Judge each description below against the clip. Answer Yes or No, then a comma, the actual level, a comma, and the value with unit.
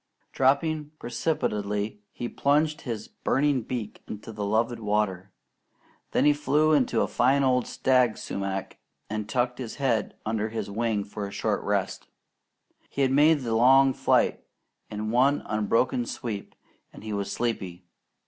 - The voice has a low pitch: Yes, low, 115 Hz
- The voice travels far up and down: No, average, 4.3 semitones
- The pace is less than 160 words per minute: Yes, average, 150 wpm